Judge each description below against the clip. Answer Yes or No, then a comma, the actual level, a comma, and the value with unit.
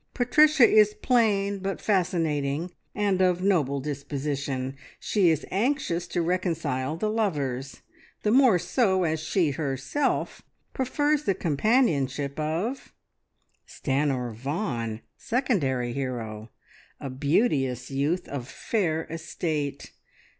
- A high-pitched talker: No, medium, 160 Hz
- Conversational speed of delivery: No, slow, 105 wpm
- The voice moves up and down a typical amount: No, wide, 6.7 semitones